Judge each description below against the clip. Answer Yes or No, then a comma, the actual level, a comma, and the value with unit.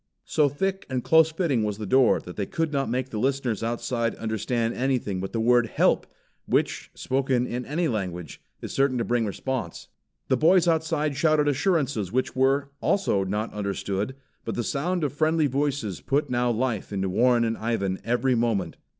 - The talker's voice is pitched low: Yes, low, 125 Hz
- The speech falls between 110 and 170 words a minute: No, average, 180 wpm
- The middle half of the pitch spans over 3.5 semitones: Yes, average, 4.4 semitones